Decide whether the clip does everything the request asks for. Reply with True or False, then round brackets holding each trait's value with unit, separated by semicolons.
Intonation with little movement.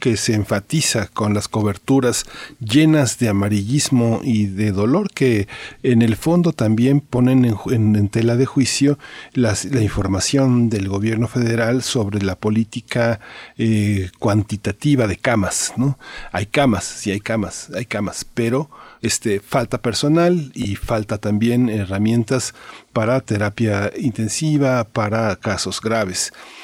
False (3.7 semitones)